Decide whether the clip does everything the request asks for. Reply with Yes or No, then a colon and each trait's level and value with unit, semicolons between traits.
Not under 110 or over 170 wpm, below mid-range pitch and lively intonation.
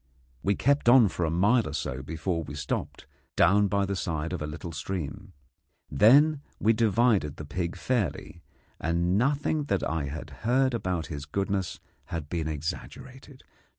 Yes: average, 160 wpm; very low, 95 Hz; wide, 6.5 semitones